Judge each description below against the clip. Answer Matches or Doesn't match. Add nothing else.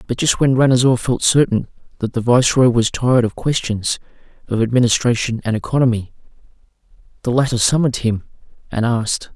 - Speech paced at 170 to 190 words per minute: Doesn't match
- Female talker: Doesn't match